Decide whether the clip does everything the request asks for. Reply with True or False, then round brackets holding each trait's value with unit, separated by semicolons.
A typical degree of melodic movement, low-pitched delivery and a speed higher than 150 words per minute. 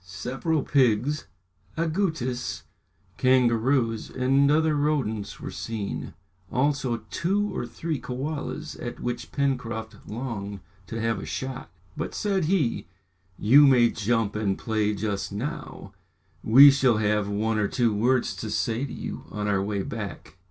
False (4.6 semitones; 120 Hz; 140 wpm)